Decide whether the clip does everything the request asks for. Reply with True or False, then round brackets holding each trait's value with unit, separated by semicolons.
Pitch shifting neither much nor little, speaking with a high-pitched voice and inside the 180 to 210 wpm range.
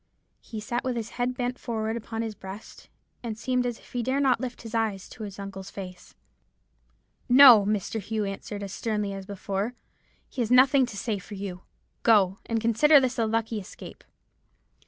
True (3.4 semitones; 225 Hz; 185 wpm)